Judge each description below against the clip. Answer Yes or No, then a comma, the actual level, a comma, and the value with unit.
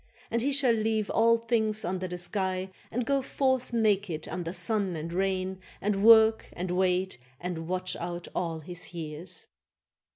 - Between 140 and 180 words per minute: Yes, average, 160 wpm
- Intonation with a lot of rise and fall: No, average, 3.9 semitones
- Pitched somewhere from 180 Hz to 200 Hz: Yes, high, 190 Hz